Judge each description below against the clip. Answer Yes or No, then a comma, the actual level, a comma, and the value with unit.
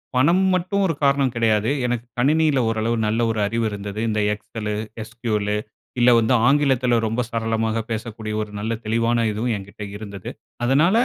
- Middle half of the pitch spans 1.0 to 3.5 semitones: Yes, average, 3.2 semitones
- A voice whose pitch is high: No, low, 115 Hz